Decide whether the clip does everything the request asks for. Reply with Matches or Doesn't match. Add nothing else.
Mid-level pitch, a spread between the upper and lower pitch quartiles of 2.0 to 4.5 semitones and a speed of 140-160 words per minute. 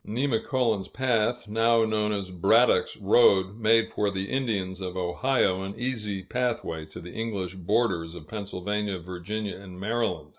Doesn't match